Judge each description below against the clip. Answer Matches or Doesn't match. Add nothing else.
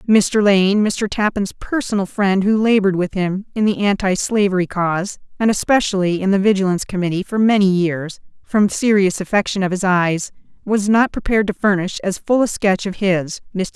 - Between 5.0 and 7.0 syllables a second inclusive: Matches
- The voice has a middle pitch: Doesn't match